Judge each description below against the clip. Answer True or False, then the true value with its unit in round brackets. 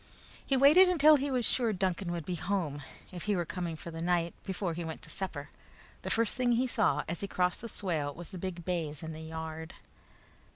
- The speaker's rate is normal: False (225 wpm)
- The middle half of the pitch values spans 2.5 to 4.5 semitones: False (5.1 semitones)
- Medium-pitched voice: True (180 Hz)